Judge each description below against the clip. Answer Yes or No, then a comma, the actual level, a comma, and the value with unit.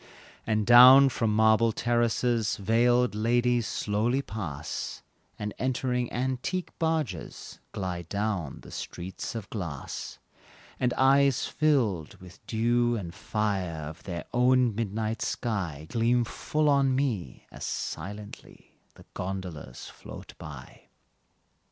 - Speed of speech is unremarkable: No, slow, 115 wpm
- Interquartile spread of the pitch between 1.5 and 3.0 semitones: No, average, 4.2 semitones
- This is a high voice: No, low, 110 Hz